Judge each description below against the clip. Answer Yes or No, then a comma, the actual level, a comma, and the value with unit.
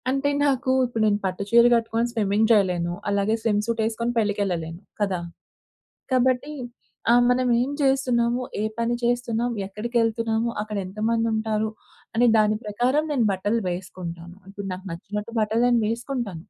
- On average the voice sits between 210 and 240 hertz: Yes, high, 225 Hz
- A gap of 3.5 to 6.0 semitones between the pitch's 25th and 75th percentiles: No, average, 2.8 semitones